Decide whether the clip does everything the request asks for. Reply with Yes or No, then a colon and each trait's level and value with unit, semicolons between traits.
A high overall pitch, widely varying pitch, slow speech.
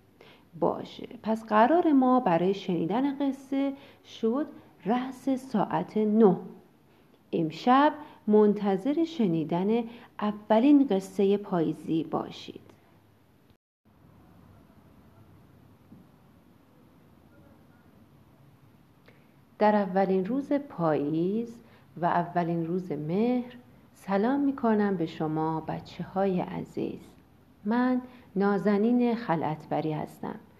Yes: high, 210 Hz; wide, 6.1 semitones; slow, 75 wpm